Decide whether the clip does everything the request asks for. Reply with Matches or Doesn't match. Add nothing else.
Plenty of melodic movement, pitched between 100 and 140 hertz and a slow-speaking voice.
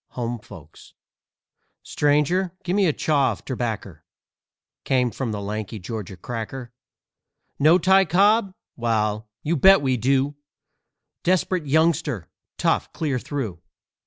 Matches